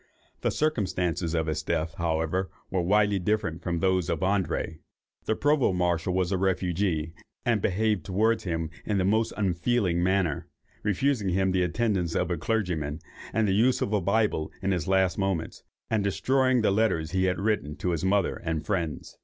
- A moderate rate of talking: Yes, average, 180 wpm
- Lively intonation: No, average, 3.6 semitones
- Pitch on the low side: Yes, very low, 95 Hz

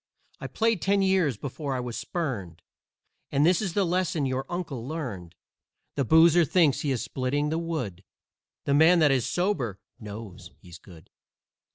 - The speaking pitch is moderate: Yes, medium, 145 Hz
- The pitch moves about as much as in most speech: No, wide, 6.7 semitones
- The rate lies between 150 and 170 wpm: Yes, average, 165 wpm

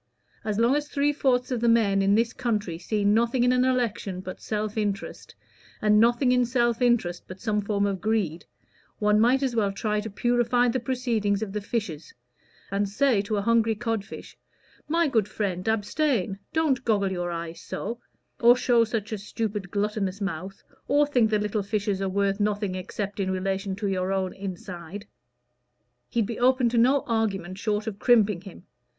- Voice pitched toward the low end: No, high, 210 Hz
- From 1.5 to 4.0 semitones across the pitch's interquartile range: Yes, average, 3.4 semitones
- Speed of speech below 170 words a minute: No, average, 185 wpm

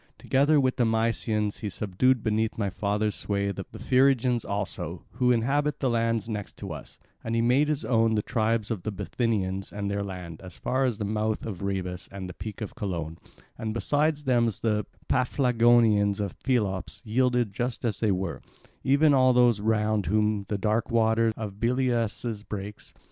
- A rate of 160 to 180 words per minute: Yes, average, 175 wpm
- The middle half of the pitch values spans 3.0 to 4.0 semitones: Yes, average, 3.3 semitones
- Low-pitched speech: Yes, low, 110 Hz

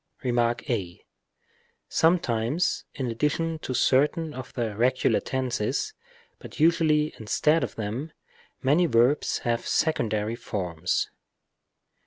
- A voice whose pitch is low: Yes, low, 130 Hz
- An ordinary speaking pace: No, slow, 105 wpm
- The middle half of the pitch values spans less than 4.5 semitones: No, average, 5.2 semitones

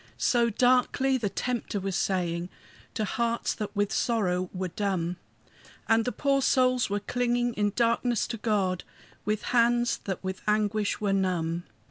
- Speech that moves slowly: No, average, 150 wpm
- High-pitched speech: Yes, high, 210 Hz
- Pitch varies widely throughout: No, average, 4.1 semitones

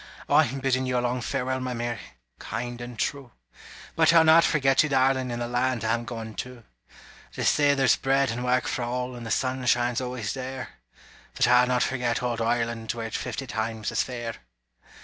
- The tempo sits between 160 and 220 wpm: Yes, average, 195 wpm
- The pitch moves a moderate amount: No, narrow, 1.7 semitones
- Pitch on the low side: Yes, low, 125 Hz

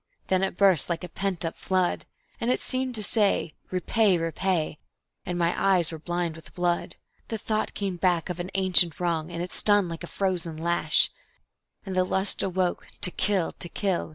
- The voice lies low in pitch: No, medium, 180 Hz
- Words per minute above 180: Yes, average, 190 wpm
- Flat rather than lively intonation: Yes, narrow, 2.2 semitones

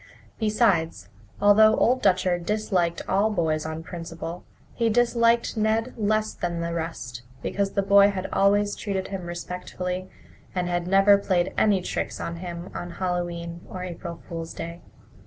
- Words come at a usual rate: Yes, average, 150 wpm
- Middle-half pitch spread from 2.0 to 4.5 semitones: Yes, average, 3.2 semitones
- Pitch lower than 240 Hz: Yes, medium, 185 Hz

